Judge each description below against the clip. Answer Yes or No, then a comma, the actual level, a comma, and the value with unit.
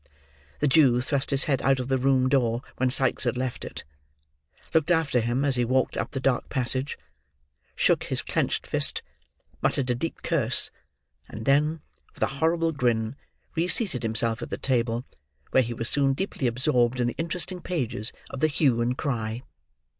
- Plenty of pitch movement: No, average, 3.1 semitones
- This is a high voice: No, low, 130 Hz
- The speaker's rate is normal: Yes, average, 175 wpm